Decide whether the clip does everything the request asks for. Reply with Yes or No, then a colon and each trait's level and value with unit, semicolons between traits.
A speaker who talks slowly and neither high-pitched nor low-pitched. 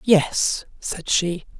Yes: slow, 115 wpm; medium, 180 Hz